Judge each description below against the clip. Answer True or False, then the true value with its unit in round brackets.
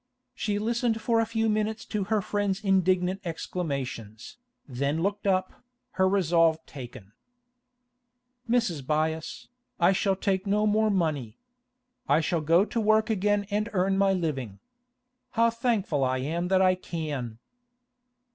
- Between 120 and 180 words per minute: True (135 wpm)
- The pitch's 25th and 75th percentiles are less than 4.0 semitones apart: False (5.1 semitones)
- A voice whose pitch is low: False (185 Hz)